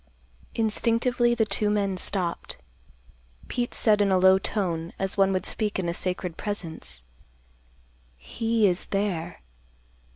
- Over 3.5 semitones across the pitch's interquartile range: No, average, 3.0 semitones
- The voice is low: No, high, 195 Hz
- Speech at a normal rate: No, slow, 130 wpm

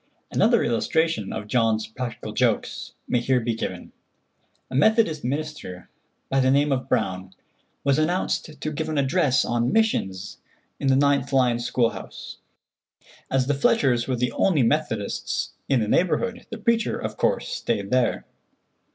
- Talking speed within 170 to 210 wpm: No, average, 150 wpm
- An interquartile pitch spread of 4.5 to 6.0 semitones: Yes, average, 4.8 semitones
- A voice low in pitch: Yes, low, 130 Hz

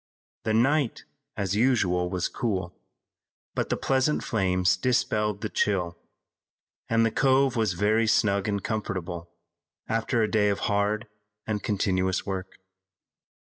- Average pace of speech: No, slow, 130 wpm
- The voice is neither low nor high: No, low, 105 Hz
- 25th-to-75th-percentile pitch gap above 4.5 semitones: No, average, 3.4 semitones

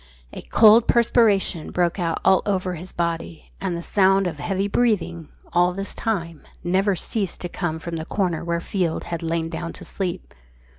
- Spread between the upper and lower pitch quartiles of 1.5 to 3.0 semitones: Yes, average, 2.7 semitones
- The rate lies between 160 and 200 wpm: Yes, average, 180 wpm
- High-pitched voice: No, medium, 175 Hz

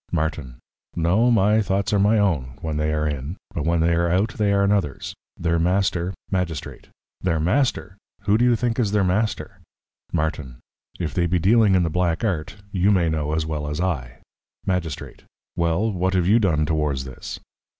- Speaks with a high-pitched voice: No, very low, 85 Hz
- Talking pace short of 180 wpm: No, average, 185 wpm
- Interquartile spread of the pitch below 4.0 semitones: No, average, 4.3 semitones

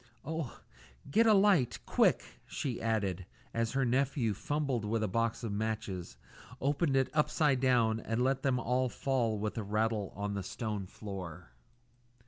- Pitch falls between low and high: No, low, 115 Hz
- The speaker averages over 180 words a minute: No, average, 160 wpm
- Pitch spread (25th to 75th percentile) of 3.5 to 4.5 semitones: Yes, average, 4.2 semitones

